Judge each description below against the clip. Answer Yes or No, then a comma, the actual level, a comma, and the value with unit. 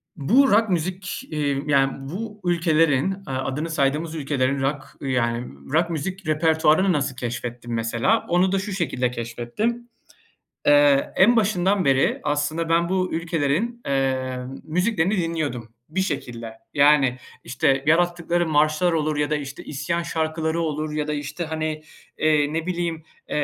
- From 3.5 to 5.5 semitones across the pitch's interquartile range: Yes, average, 4.1 semitones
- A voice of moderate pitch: Yes, medium, 155 Hz